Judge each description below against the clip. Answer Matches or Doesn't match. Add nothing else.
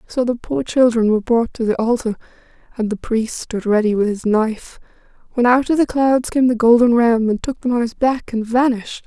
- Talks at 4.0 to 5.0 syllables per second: Doesn't match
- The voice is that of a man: Doesn't match